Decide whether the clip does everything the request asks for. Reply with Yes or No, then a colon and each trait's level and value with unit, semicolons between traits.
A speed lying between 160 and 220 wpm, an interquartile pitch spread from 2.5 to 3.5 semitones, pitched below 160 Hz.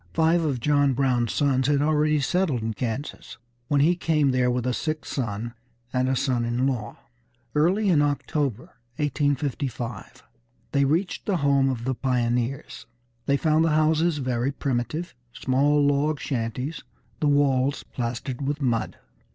No: average, 150 wpm; average, 3.2 semitones; medium, 140 Hz